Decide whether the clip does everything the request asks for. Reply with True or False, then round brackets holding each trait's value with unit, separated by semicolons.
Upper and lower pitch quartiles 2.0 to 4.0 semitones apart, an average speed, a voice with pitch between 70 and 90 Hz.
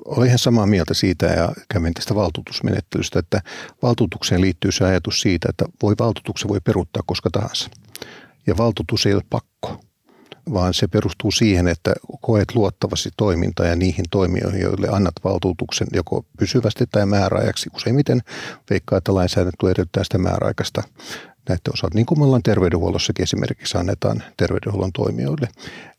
False (3.3 semitones; 145 wpm; 100 Hz)